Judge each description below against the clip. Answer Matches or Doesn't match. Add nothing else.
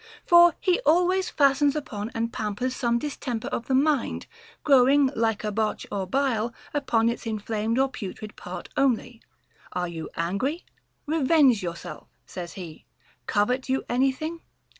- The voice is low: Doesn't match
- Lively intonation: Doesn't match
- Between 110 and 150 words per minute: Matches